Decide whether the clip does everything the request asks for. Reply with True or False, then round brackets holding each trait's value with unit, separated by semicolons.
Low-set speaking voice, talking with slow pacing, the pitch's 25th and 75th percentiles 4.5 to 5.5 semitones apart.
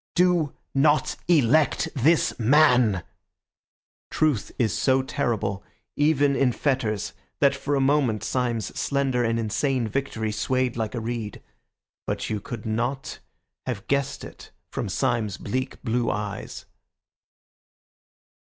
False (125 Hz; 120 wpm; 3.9 semitones)